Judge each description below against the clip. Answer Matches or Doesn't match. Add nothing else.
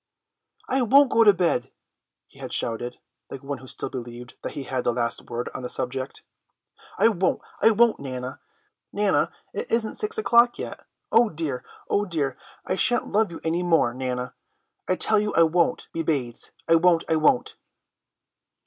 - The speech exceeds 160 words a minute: Matches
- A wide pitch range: Matches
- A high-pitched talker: Doesn't match